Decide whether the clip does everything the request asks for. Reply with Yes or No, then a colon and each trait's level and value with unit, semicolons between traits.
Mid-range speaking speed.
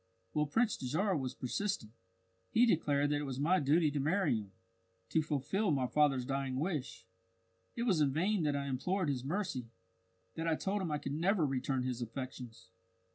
Yes: average, 185 wpm